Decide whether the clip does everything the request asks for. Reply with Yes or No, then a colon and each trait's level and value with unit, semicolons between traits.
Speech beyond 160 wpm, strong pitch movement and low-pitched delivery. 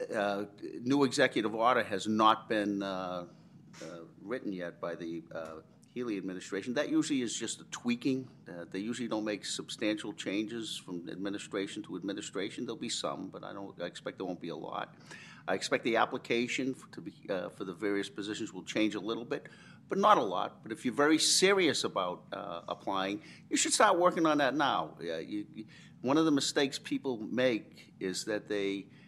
Yes: average, 200 wpm; wide, 6.5 semitones; low, 115 Hz